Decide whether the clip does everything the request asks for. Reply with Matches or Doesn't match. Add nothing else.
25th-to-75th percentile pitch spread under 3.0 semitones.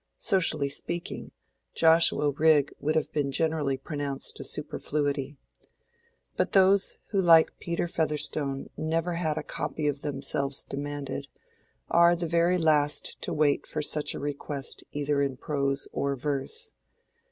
Matches